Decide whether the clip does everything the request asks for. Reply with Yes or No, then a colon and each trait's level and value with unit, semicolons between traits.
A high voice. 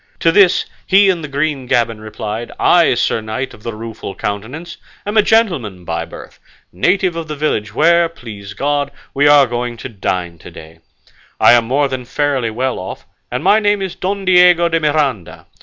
No: medium, 140 Hz